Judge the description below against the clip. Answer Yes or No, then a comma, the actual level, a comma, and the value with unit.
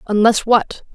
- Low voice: No, high, 220 Hz